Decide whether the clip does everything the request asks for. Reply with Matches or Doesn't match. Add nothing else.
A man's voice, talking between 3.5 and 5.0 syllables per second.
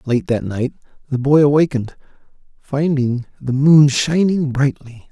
Matches